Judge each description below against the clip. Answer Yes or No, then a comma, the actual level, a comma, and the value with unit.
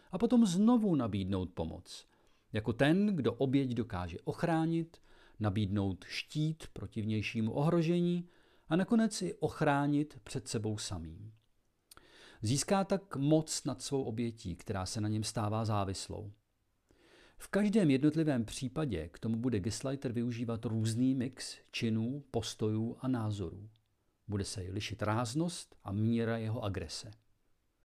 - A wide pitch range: Yes, wide, 5.8 semitones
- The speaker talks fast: No, average, 125 wpm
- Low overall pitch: Yes, low, 115 Hz